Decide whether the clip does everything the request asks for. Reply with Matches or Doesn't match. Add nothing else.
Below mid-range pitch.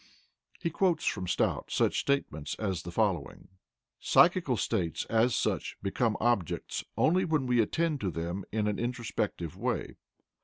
Matches